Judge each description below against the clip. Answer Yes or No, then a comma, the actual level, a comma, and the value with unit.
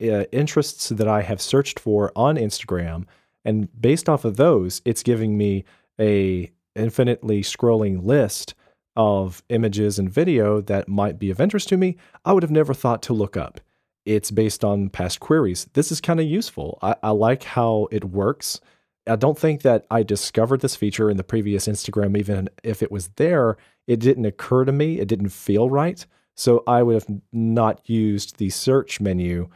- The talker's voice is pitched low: Yes, low, 110 Hz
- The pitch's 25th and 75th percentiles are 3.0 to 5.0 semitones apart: Yes, average, 4.1 semitones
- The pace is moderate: Yes, average, 185 wpm